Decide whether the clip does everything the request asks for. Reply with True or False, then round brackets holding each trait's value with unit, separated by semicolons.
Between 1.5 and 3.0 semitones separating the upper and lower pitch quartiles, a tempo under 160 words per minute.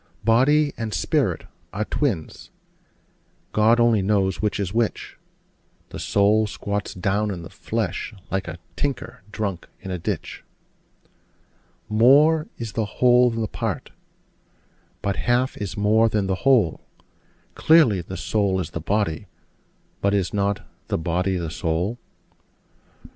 False (3.4 semitones; 135 wpm)